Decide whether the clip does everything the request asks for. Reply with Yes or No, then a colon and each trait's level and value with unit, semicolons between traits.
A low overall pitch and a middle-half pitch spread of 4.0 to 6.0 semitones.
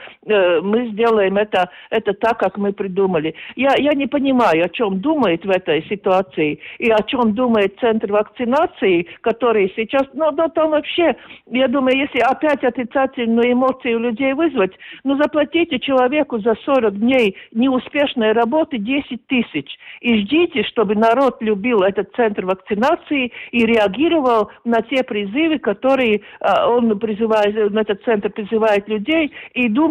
No: high, 235 Hz; average, 4.3 semitones